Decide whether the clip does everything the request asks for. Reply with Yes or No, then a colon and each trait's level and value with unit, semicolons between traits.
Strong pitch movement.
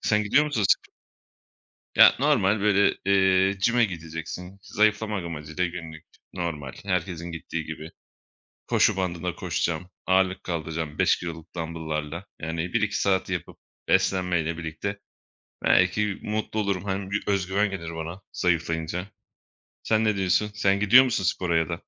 No: average, 3.3 semitones